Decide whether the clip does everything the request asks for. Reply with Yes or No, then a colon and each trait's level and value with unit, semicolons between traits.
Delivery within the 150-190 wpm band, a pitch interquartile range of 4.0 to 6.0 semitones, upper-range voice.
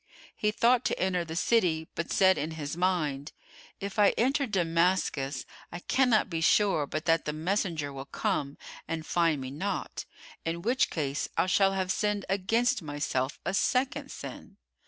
No: average, 165 wpm; average, 4.7 semitones; medium, 175 Hz